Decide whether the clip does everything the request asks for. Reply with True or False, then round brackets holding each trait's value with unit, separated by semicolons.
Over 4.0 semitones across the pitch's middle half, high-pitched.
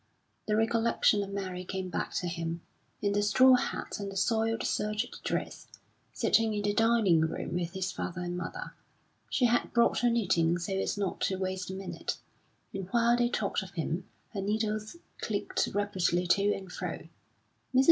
False (3.4 semitones; 200 Hz)